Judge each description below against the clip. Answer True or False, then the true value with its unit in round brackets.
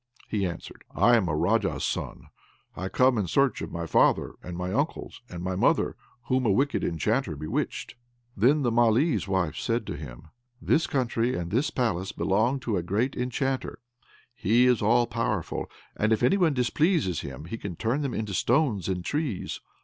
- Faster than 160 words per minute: True (180 wpm)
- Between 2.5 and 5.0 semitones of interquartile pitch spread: False (5.5 semitones)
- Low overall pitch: True (115 Hz)